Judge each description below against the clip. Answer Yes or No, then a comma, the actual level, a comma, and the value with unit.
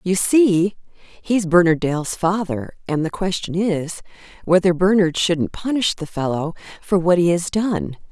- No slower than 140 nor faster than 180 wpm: Yes, average, 155 wpm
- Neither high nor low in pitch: Yes, medium, 180 Hz